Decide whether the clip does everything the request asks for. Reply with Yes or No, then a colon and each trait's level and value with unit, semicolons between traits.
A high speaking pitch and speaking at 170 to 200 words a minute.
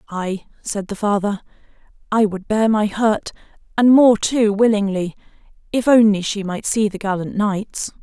No: high, 210 Hz; average, 155 wpm